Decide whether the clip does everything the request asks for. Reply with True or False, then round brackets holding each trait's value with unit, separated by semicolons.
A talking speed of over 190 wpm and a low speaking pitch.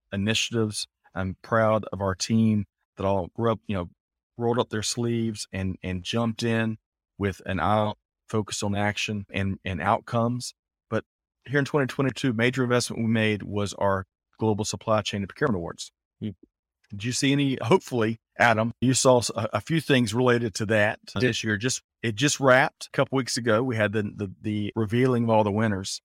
False (185 wpm; 110 Hz)